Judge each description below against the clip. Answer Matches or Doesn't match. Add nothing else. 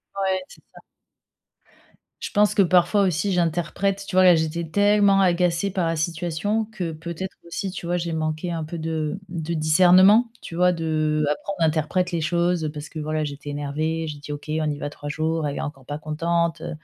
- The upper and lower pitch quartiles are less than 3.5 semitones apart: Matches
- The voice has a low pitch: Doesn't match